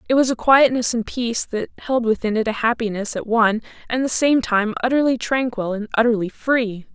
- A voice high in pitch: Yes, high, 235 Hz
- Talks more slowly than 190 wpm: No, average, 200 wpm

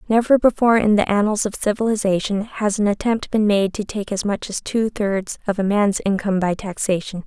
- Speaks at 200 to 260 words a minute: Yes, fast, 205 wpm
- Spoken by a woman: Yes, female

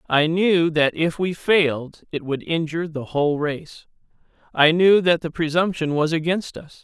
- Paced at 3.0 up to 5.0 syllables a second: Yes, 4.6 syllables/s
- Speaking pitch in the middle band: Yes, medium, 160 Hz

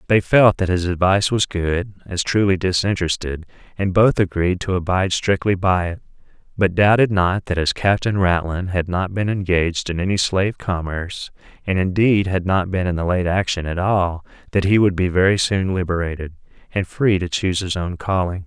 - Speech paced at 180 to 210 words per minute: Yes, average, 190 wpm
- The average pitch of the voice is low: Yes, very low, 95 Hz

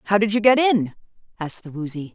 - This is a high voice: Yes, high, 195 Hz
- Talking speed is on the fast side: Yes, fast, 225 wpm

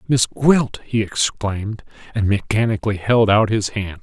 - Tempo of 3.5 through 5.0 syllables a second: Yes, 4.5 syllables/s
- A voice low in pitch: Yes, low, 110 Hz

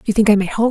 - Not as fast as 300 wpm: No, fast, 425 wpm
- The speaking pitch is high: Yes, high, 215 Hz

